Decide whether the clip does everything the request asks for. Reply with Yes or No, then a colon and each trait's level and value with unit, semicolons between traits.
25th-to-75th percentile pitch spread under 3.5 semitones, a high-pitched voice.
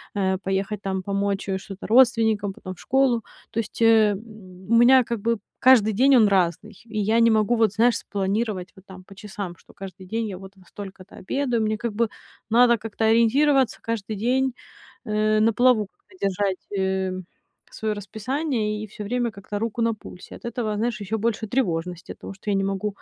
Yes: average, 3.0 semitones; high, 215 Hz